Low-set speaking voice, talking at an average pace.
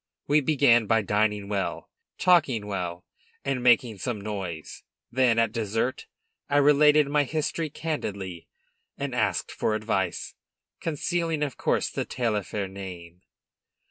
No: low, 115 Hz; slow, 125 wpm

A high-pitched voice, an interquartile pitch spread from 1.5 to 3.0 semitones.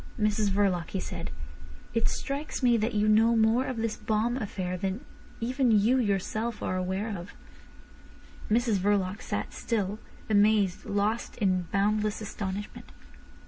Yes: high, 210 Hz; narrow, 2.6 semitones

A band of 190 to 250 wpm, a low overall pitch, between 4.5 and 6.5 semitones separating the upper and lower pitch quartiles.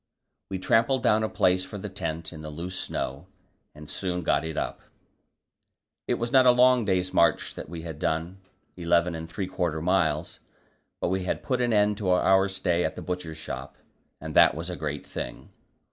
No: average, 195 wpm; very low, 90 Hz; average, 3.3 semitones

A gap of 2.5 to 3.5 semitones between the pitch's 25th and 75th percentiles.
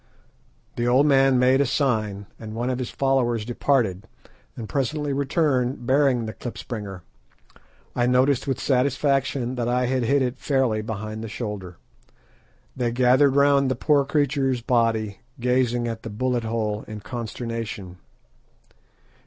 Yes: average, 3.2 semitones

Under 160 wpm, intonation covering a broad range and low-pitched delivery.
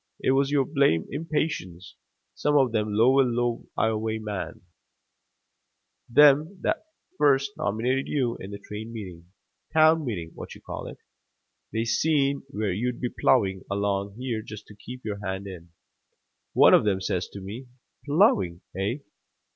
Yes: average, 145 wpm; wide, 5.7 semitones; low, 110 Hz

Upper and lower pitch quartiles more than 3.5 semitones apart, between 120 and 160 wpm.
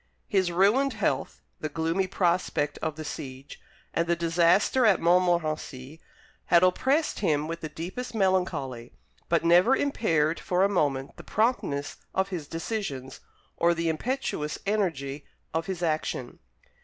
Yes: average, 4.1 semitones; average, 140 wpm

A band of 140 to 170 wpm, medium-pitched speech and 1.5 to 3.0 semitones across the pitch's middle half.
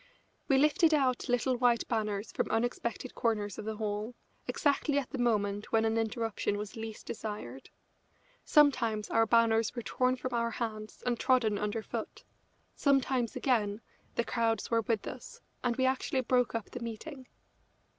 No: average, 160 wpm; high, 230 Hz; average, 2.7 semitones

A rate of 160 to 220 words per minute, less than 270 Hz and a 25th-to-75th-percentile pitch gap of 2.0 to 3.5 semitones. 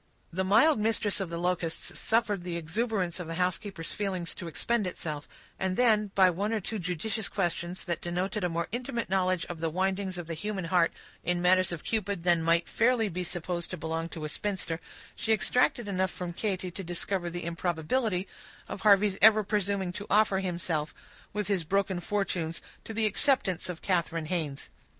Yes: average, 185 wpm; medium, 185 Hz; average, 3.2 semitones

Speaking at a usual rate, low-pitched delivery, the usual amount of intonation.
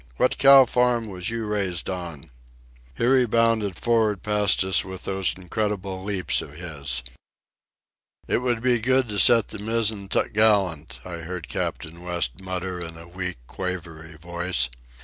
Yes: average, 150 wpm; very low, 95 Hz; average, 4.3 semitones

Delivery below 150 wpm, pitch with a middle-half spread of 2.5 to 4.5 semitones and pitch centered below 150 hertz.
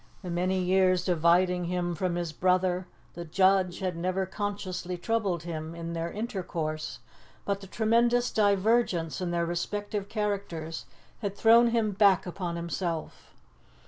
No: average, 140 wpm; average, 2.8 semitones; medium, 185 Hz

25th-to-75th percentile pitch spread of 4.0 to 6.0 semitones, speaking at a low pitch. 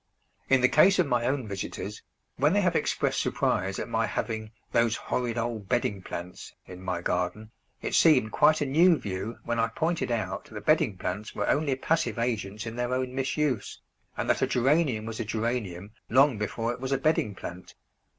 Yes: average, 4.3 semitones; low, 115 Hz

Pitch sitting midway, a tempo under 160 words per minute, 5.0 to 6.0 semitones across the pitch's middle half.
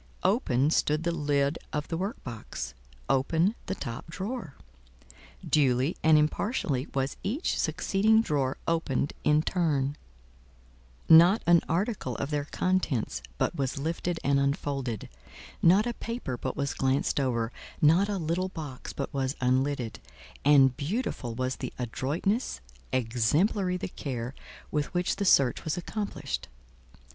Yes: medium, 150 Hz; slow, 135 wpm; average, 5.3 semitones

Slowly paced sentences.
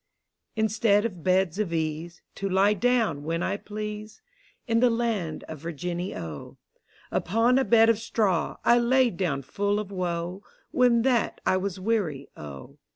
No: average, 155 wpm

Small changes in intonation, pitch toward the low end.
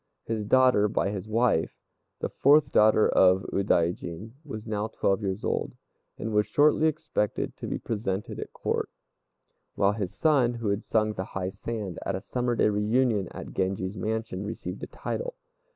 No: average, 3.3 semitones; low, 105 Hz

